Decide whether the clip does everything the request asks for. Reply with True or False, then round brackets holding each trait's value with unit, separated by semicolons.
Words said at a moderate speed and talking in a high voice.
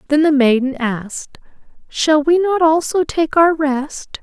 True (155 wpm; 300 Hz)